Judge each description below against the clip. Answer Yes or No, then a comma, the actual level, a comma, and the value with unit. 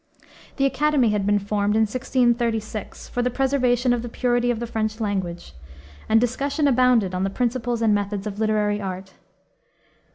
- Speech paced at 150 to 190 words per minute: Yes, average, 165 wpm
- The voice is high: Yes, high, 225 Hz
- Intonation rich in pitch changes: No, average, 3.1 semitones